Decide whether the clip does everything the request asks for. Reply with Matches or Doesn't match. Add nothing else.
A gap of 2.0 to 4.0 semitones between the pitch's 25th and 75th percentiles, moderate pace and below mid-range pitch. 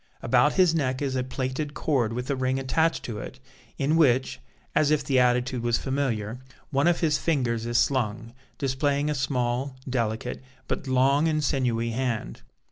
Matches